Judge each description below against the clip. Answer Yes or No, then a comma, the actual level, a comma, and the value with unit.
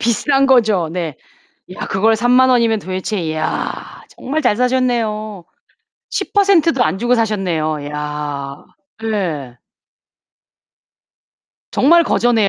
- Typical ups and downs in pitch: No, wide, 6.7 semitones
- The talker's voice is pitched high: Yes, high, 215 Hz